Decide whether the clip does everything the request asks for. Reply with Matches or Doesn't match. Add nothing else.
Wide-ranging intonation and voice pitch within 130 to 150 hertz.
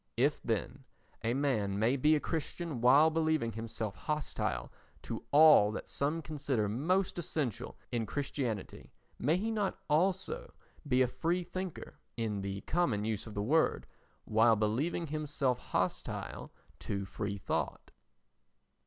Matches